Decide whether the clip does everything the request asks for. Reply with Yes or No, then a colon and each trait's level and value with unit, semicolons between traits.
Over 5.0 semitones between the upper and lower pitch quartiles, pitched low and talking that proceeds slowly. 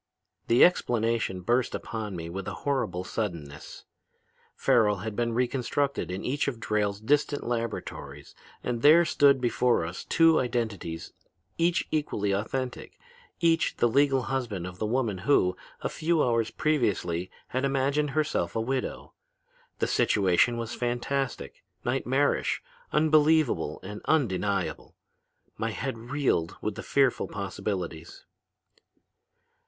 Yes: wide, 5.5 semitones; low, 120 Hz; slow, 125 wpm